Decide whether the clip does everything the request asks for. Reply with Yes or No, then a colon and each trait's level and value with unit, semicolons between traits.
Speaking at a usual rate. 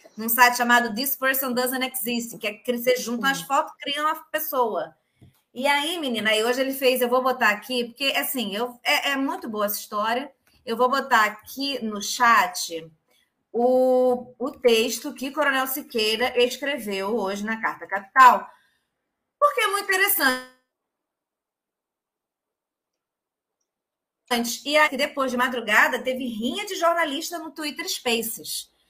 Yes: average, 145 wpm